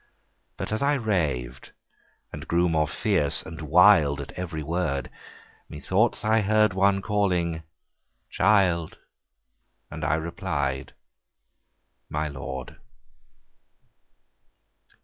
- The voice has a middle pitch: No, very low, 85 Hz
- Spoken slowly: Yes, slow, 100 wpm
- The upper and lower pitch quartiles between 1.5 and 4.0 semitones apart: No, average, 5.0 semitones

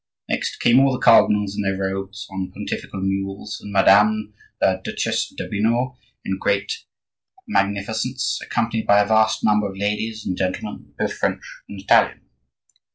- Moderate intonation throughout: No, narrow, 2.1 semitones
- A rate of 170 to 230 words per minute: No, average, 150 wpm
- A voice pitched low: Yes, low, 100 Hz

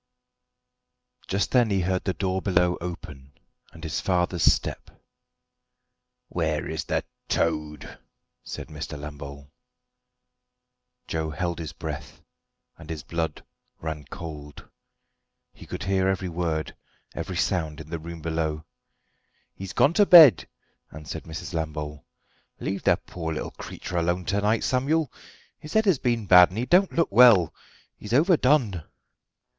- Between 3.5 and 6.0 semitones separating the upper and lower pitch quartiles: Yes, average, 4.5 semitones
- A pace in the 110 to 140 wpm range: Yes, slow, 135 wpm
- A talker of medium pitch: No, very low, 85 Hz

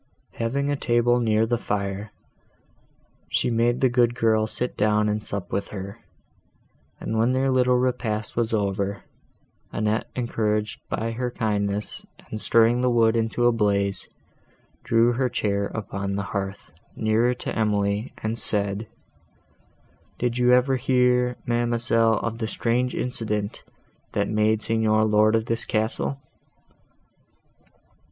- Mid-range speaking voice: No, low, 110 Hz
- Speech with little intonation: Yes, narrow, 2.3 semitones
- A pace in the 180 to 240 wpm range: No, slow, 135 wpm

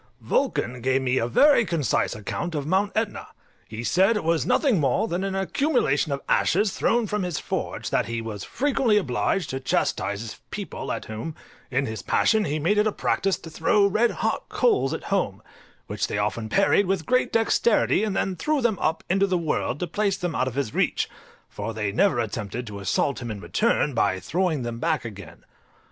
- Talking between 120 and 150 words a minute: No, average, 200 wpm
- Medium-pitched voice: Yes, medium, 165 Hz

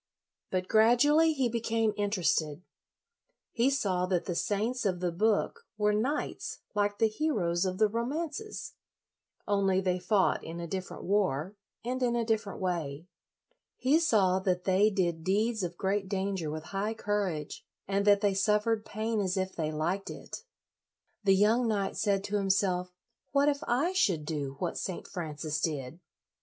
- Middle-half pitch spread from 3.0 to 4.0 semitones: Yes, average, 3.6 semitones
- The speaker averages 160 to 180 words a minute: Yes, average, 165 wpm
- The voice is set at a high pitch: Yes, high, 200 Hz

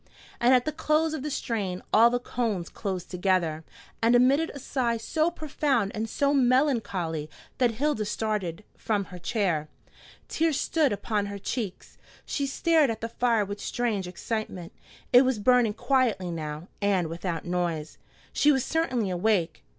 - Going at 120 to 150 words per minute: No, average, 160 wpm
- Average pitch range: No, wide, 6.0 semitones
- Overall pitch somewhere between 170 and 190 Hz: No, high, 220 Hz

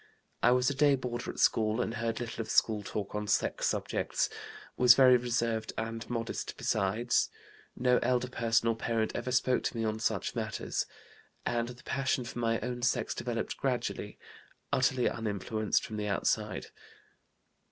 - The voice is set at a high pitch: No, low, 115 Hz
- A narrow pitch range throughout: Yes, narrow, 2.0 semitones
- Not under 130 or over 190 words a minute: Yes, average, 165 wpm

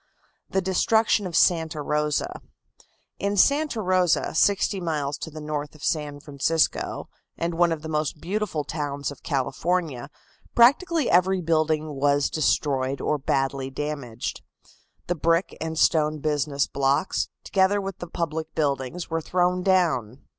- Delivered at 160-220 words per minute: No, average, 140 wpm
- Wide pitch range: No, average, 3.9 semitones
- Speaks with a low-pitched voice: No, medium, 160 Hz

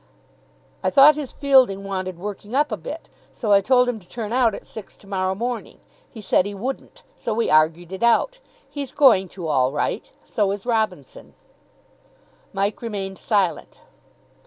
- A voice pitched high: Yes, high, 210 Hz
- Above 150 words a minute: Yes, average, 170 wpm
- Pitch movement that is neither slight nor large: Yes, average, 4.5 semitones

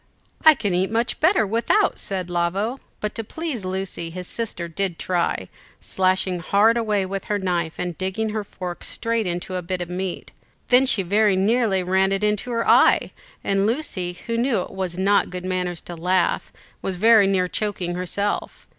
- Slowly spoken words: No, average, 180 wpm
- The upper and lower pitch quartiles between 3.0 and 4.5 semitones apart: Yes, average, 3.3 semitones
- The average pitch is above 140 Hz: Yes, high, 190 Hz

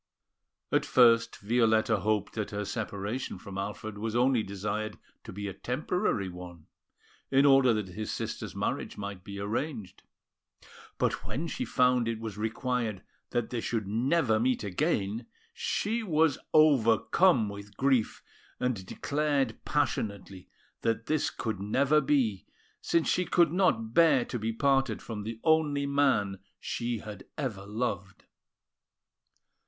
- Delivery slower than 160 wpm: Yes, average, 140 wpm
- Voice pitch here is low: Yes, low, 115 Hz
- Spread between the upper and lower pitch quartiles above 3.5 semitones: Yes, average, 5.1 semitones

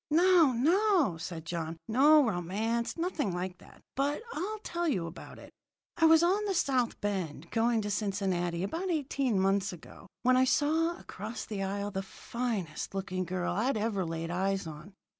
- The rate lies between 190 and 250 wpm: No, average, 170 wpm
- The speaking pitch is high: Yes, high, 215 Hz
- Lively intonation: Yes, wide, 8.0 semitones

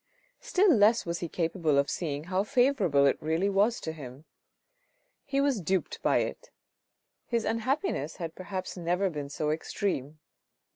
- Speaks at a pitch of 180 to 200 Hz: Yes, medium, 185 Hz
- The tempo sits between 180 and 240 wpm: No, average, 150 wpm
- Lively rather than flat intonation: Yes, wide, 6.4 semitones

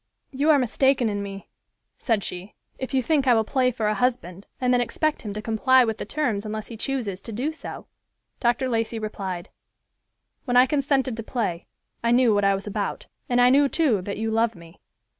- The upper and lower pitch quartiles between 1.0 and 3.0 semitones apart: No, average, 3.8 semitones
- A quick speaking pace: Yes, fast, 210 wpm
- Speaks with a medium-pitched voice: No, high, 230 Hz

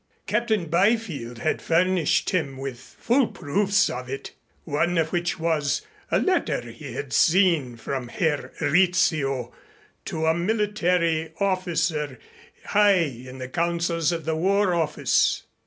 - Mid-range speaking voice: Yes, medium, 165 Hz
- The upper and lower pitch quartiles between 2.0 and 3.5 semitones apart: No, average, 4.3 semitones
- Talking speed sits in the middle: No, slow, 130 wpm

